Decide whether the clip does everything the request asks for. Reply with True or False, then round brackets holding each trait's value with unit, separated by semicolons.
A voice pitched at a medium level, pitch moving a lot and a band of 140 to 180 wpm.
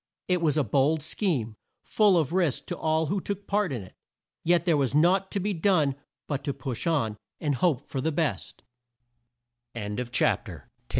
False (160 Hz; 4.8 semitones; 170 wpm)